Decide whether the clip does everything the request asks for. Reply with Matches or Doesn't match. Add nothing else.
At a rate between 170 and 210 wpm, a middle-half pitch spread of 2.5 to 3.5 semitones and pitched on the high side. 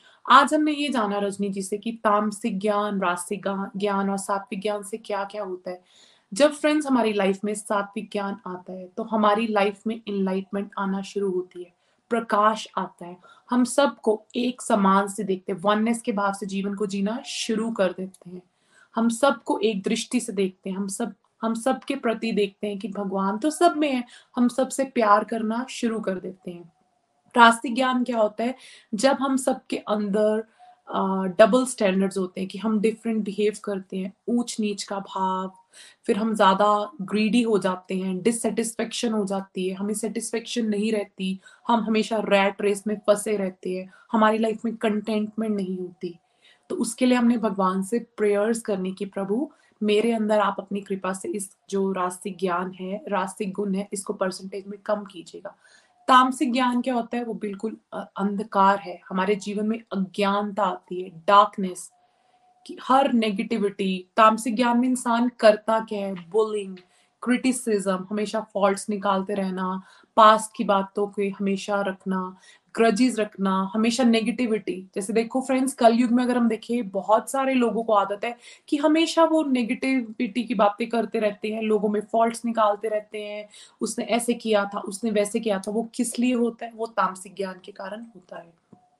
Matches